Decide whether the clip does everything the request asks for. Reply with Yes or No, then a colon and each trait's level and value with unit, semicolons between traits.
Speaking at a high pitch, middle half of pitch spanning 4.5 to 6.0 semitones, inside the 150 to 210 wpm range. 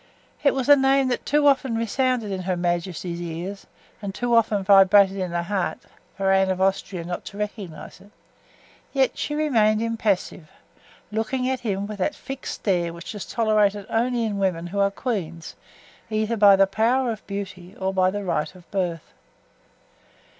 No: high, 200 Hz; average, 3.7 semitones; average, 175 wpm